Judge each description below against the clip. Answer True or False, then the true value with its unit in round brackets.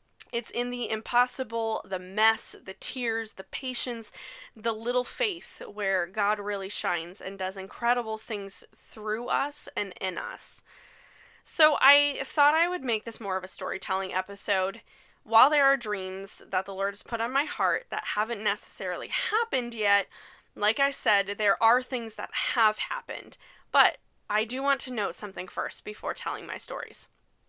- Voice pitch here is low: False (225 Hz)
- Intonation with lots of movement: False (4.6 semitones)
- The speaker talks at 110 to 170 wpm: True (165 wpm)